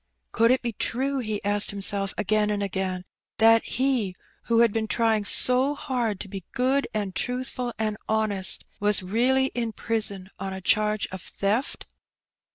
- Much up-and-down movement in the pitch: No, average, 3.2 semitones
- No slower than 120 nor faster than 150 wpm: No, average, 165 wpm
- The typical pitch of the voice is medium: No, high, 215 Hz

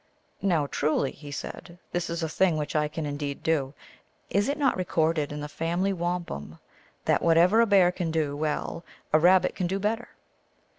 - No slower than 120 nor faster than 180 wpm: No, average, 200 wpm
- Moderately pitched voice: Yes, medium, 165 Hz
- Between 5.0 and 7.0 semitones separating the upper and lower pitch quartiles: No, average, 3.5 semitones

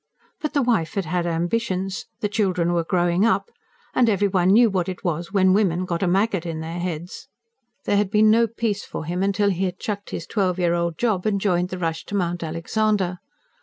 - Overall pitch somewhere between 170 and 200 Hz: Yes, medium, 185 Hz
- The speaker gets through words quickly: Yes, fast, 215 wpm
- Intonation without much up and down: No, average, 3.1 semitones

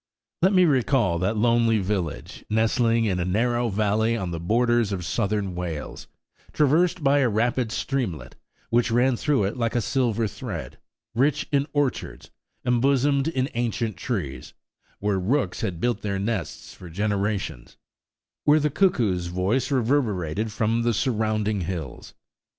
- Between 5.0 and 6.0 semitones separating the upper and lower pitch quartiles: No, average, 4.5 semitones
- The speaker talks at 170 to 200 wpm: No, average, 140 wpm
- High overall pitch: No, low, 115 Hz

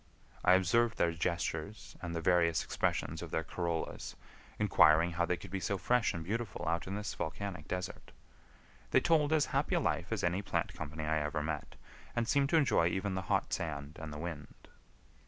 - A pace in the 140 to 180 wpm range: No, average, 190 wpm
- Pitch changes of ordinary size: Yes, average, 3.8 semitones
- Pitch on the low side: Yes, very low, 85 Hz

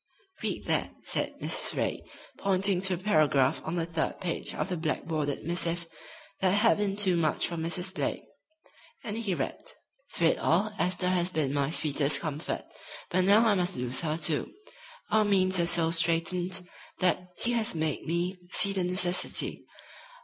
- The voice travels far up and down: No, average, 2.8 semitones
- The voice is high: No, medium, 175 Hz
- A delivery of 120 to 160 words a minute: No, average, 170 wpm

